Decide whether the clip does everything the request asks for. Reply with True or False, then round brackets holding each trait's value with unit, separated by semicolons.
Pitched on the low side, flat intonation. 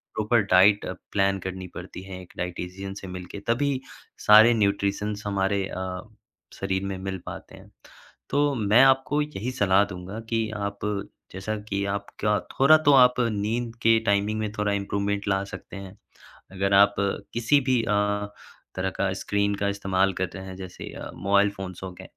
True (100 Hz; 2.1 semitones)